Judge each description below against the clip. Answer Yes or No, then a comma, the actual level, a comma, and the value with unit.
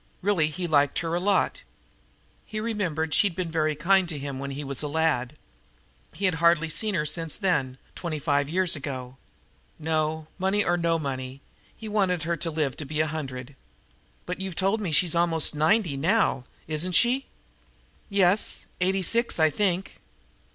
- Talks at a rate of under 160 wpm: No, average, 170 wpm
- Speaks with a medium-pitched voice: Yes, medium, 165 Hz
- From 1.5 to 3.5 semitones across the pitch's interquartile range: No, average, 3.9 semitones